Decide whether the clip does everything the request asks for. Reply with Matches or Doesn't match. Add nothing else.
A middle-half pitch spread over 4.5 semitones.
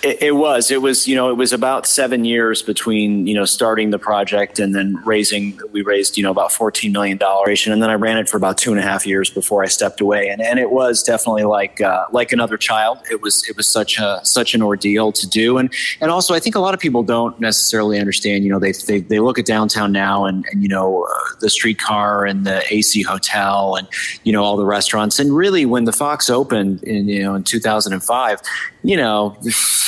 Doesn't match